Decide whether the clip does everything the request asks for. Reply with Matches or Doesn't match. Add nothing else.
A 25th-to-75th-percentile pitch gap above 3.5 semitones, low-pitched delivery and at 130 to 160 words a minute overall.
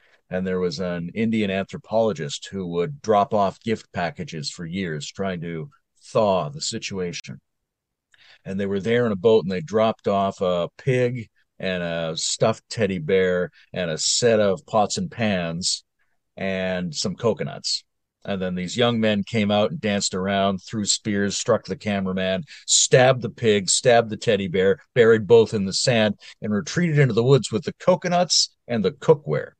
Doesn't match